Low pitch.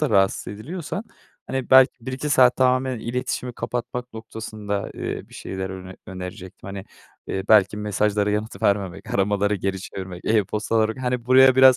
Yes: low, 110 Hz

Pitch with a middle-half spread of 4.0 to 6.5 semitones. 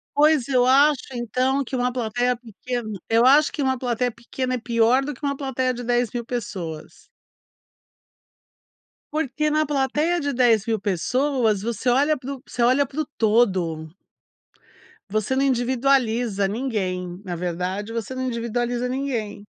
No: average, 3.4 semitones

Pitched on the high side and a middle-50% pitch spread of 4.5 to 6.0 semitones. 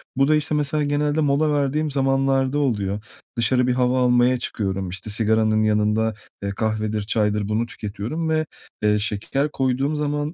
No: low, 125 Hz; average, 5.3 semitones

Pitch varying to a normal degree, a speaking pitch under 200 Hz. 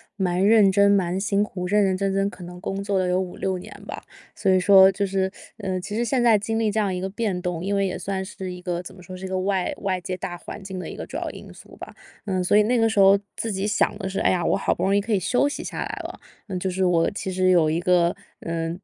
No: narrow, 1.9 semitones; high, 190 Hz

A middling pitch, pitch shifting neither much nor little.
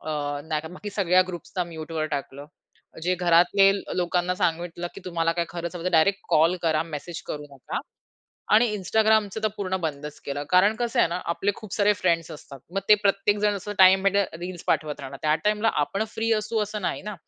Yes: medium, 180 Hz; average, 3.6 semitones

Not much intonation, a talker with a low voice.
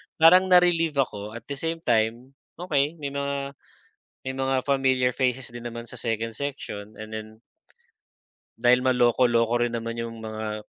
No: average, 3.4 semitones; low, 125 Hz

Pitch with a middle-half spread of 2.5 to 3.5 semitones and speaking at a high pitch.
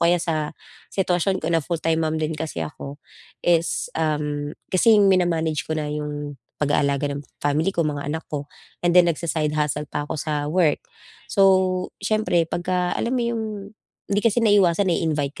No: average, 3.2 semitones; medium, 160 Hz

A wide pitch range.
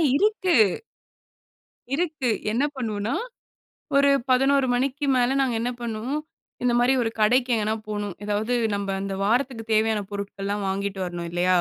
No: average, 4.3 semitones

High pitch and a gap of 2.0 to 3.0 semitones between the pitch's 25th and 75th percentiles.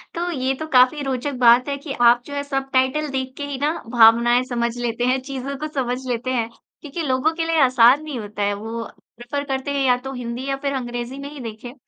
Yes: very high, 260 Hz; average, 2.7 semitones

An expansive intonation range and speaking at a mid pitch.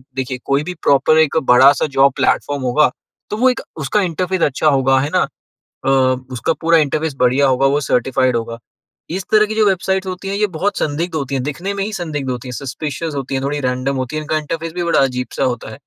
No: average, 4.5 semitones; medium, 145 Hz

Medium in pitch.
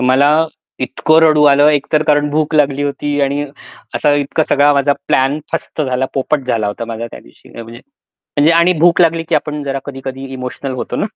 Yes: medium, 145 Hz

